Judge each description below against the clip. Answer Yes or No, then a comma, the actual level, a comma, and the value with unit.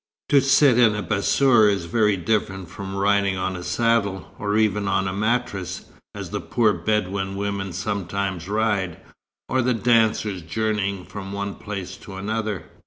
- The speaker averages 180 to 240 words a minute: No, average, 160 wpm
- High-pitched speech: No, low, 100 Hz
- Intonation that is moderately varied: No, narrow, 2.2 semitones